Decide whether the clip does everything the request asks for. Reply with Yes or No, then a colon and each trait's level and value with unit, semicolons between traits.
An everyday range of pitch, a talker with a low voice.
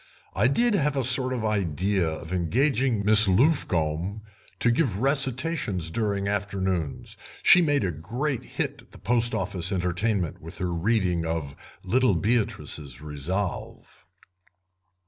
No: wide, 6.5 semitones; low, 100 Hz